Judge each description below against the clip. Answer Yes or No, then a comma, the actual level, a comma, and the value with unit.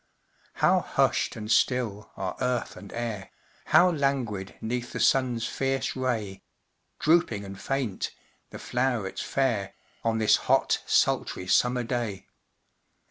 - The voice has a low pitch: Yes, low, 120 Hz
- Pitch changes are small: No, average, 3.9 semitones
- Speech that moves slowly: Yes, slow, 125 wpm